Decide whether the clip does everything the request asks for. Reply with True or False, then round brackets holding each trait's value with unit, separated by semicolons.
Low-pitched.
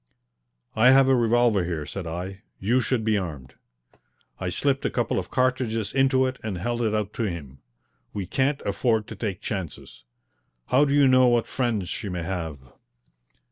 True (110 Hz)